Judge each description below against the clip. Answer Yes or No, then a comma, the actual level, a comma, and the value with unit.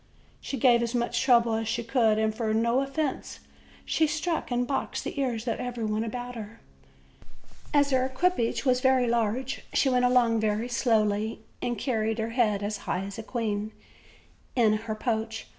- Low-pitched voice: No, high, 235 Hz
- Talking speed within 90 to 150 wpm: No, average, 175 wpm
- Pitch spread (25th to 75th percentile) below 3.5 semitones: Yes, narrow, 2.5 semitones